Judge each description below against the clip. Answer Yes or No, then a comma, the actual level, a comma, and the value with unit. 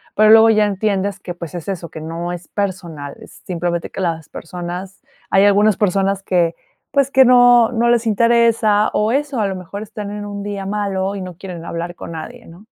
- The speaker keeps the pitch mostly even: No, average, 3.6 semitones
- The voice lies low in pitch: No, high, 195 Hz